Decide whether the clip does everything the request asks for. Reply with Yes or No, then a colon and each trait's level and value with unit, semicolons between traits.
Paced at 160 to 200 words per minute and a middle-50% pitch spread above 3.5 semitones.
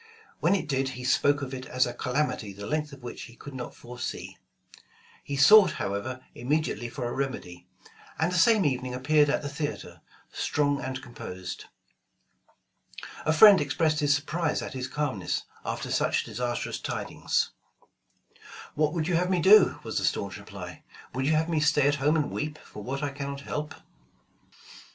No: average, 175 wpm; average, 3.2 semitones